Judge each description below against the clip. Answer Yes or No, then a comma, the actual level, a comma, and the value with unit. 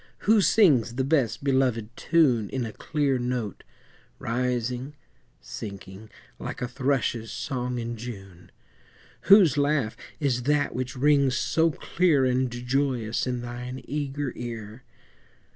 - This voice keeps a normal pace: No, slow, 125 wpm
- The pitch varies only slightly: No, average, 3.2 semitones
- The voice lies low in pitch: Yes, low, 125 Hz